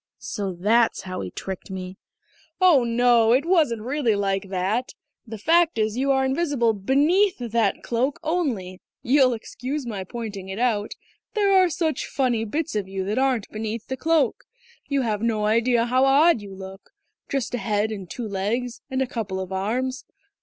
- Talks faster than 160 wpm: Yes, average, 175 wpm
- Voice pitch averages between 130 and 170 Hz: No, high, 235 Hz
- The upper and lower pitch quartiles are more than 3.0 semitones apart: Yes, average, 4.6 semitones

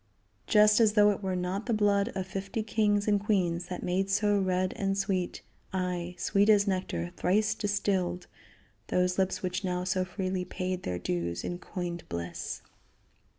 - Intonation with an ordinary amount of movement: No, narrow, 2.2 semitones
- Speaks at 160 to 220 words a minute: Yes, average, 165 wpm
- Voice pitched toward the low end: No, high, 190 Hz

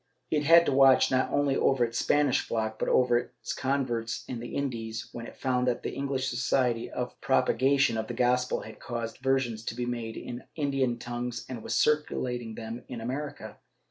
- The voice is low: Yes, low, 125 Hz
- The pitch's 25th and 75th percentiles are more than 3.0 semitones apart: No, narrow, 2.4 semitones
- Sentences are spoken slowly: No, fast, 205 wpm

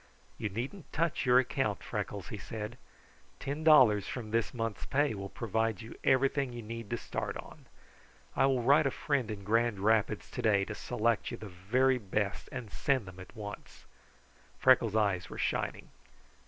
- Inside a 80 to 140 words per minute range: No, average, 170 wpm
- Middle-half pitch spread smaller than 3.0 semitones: No, average, 3.8 semitones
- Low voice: Yes, low, 115 Hz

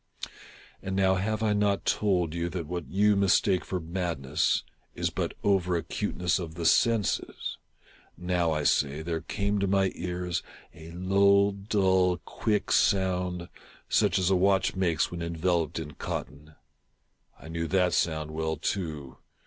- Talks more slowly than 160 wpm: Yes, average, 150 wpm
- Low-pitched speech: Yes, very low, 90 Hz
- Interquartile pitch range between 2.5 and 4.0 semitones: Yes, average, 2.9 semitones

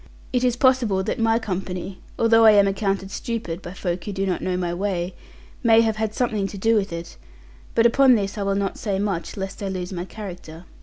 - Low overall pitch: No, high, 200 Hz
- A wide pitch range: No, average, 3.2 semitones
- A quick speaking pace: Yes, fast, 220 wpm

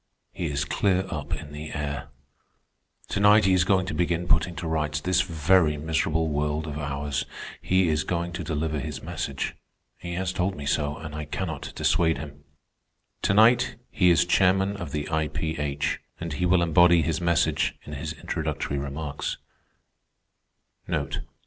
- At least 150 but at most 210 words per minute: Yes, average, 160 wpm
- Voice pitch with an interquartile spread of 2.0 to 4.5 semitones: Yes, average, 3.2 semitones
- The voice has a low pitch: Yes, very low, 80 Hz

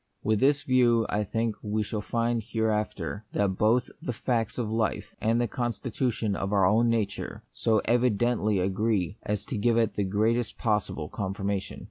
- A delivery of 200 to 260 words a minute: No, average, 175 wpm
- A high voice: No, low, 110 Hz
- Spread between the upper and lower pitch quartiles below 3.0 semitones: Yes, narrow, 2.5 semitones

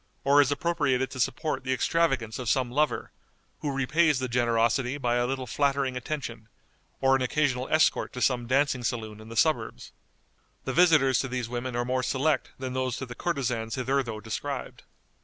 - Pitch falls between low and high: No, low, 130 Hz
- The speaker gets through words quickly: No, average, 175 wpm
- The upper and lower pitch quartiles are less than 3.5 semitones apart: Yes, narrow, 2.5 semitones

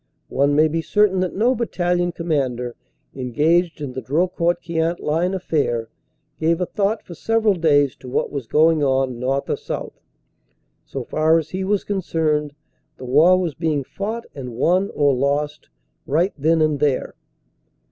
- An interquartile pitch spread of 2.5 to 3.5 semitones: No, average, 4.0 semitones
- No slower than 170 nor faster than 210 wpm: No, average, 160 wpm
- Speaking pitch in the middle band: Yes, medium, 160 Hz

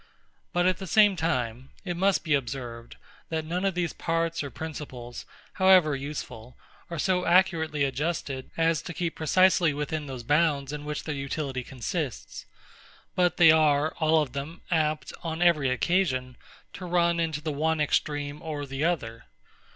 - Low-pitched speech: No, medium, 155 Hz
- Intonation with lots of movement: No, average, 3.6 semitones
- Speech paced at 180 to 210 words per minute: No, average, 160 wpm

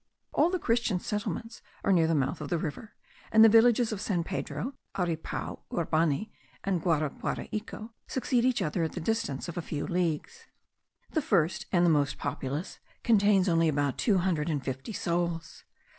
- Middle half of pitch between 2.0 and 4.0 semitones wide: No, wide, 5.5 semitones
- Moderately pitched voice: Yes, medium, 175 Hz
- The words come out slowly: No, average, 170 wpm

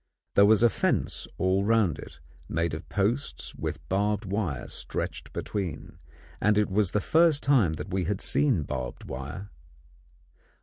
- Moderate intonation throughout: Yes, average, 3.9 semitones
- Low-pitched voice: Yes, low, 100 Hz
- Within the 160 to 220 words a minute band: No, average, 150 wpm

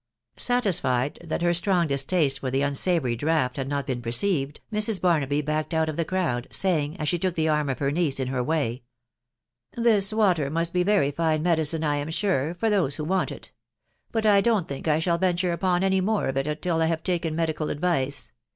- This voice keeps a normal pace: No, fast, 210 wpm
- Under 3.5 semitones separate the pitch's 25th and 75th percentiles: No, average, 4.1 semitones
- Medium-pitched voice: Yes, medium, 160 Hz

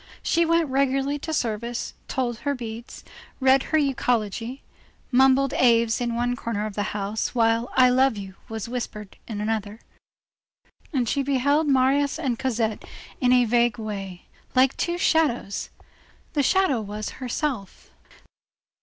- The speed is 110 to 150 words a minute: Yes, average, 145 wpm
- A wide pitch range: No, average, 3.6 semitones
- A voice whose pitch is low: No, high, 245 Hz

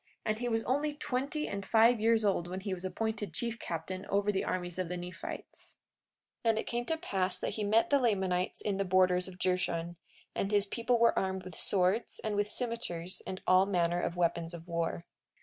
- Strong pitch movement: No, average, 3.9 semitones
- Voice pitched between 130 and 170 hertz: No, high, 195 Hz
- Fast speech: Yes, fast, 210 wpm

